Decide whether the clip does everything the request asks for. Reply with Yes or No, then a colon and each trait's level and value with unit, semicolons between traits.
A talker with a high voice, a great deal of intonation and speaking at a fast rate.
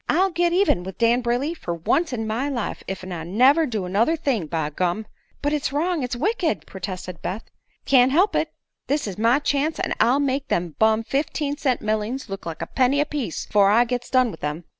Yes: high, 245 Hz; wide, 6.7 semitones; fast, 215 wpm